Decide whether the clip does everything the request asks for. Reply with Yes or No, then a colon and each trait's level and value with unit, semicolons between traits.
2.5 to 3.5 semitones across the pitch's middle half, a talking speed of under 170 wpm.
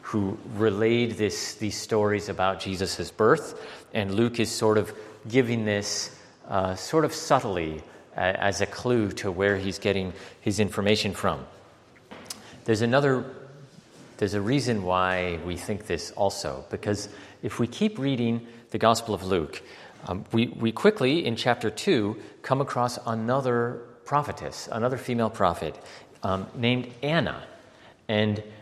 Yes: average, 3.1 semitones; average, 140 wpm